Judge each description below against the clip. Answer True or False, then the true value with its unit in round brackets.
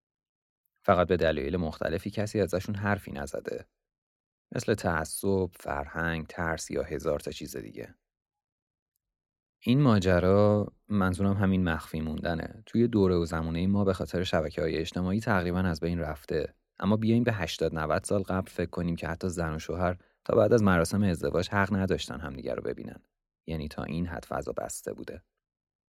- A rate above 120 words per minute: True (155 wpm)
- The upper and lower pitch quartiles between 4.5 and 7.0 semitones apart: False (3.5 semitones)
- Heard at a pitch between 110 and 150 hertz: False (90 Hz)